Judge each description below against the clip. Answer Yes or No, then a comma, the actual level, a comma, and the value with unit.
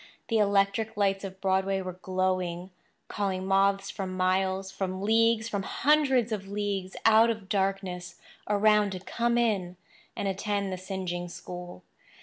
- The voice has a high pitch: Yes, high, 195 Hz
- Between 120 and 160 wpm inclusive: Yes, slow, 135 wpm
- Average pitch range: No, narrow, 2.0 semitones